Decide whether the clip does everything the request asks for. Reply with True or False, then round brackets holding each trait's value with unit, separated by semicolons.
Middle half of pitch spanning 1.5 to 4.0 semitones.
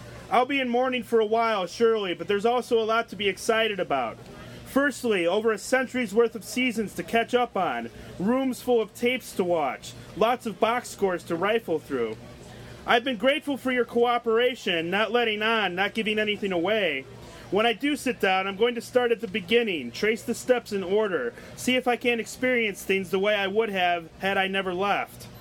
True (3.7 semitones)